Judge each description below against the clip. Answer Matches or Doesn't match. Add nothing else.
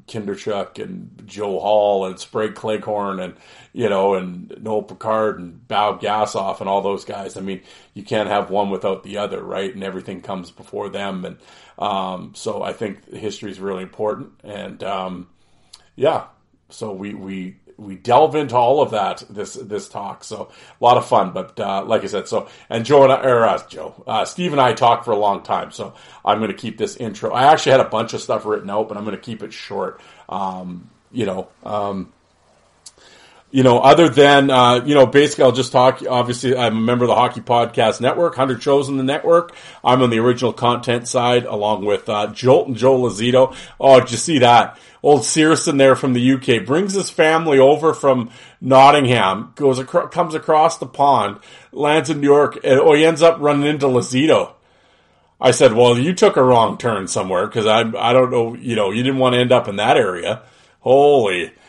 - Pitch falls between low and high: Doesn't match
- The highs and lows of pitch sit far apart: Doesn't match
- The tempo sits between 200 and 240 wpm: Matches